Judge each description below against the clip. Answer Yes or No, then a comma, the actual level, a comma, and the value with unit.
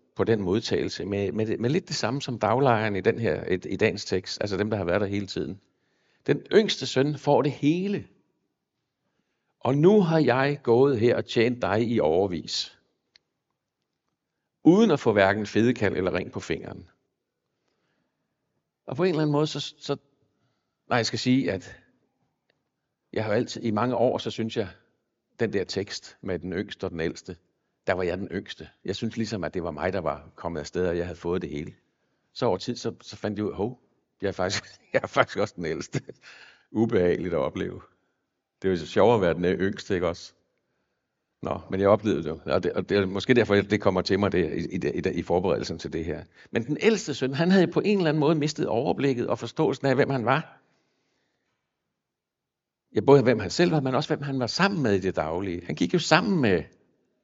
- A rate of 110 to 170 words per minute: No, average, 210 wpm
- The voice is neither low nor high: No, low, 120 Hz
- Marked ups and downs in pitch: Yes, wide, 5.7 semitones